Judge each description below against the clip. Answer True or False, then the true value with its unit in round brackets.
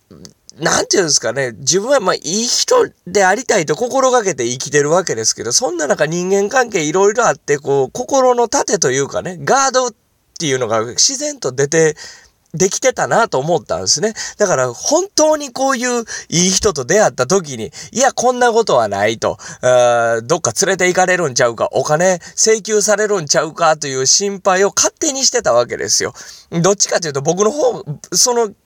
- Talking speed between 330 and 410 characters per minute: True (375 characters per minute)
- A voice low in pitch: False (195 Hz)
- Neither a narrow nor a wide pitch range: False (7.8 semitones)